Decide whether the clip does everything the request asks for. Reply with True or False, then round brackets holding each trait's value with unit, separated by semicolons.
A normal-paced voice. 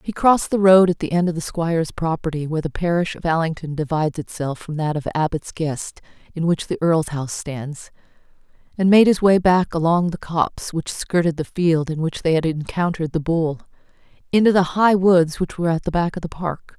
False (215 wpm)